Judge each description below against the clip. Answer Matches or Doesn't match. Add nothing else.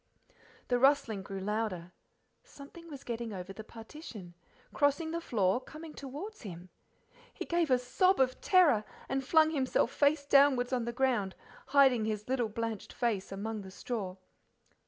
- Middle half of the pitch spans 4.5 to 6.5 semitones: Matches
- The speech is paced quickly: Doesn't match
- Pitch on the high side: Matches